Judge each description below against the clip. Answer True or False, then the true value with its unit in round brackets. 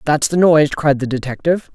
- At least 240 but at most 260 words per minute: False (205 wpm)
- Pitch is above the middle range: False (150 Hz)